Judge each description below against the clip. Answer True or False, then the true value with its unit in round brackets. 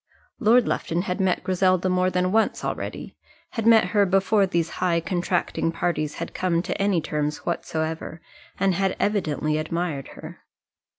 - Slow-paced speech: False (155 wpm)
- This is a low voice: False (180 Hz)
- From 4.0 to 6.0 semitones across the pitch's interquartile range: False (2.7 semitones)